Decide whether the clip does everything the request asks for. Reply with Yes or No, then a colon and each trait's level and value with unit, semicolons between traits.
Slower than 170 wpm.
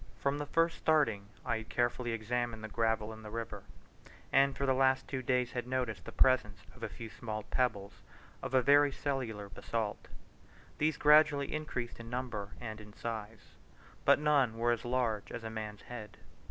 No: average, 180 wpm